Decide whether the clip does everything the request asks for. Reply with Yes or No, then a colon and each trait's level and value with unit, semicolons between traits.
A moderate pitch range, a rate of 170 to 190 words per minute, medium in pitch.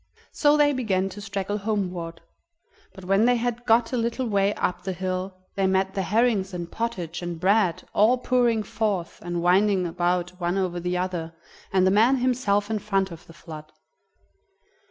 No: average, 3.8 semitones; average, 175 wpm; high, 195 Hz